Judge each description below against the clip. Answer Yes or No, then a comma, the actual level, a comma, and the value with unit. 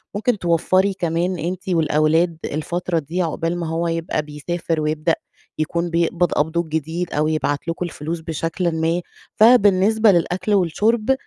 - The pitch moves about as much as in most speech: No, narrow, 2.2 semitones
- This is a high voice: No, medium, 170 Hz